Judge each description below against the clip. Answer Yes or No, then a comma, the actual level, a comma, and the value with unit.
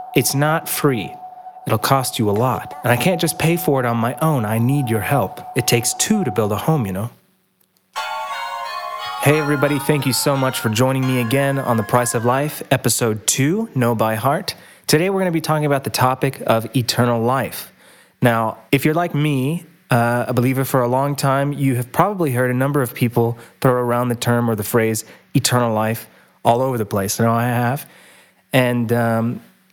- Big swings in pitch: No, average, 3.6 semitones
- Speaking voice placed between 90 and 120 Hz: No, low, 130 Hz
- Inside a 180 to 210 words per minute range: Yes, fast, 205 wpm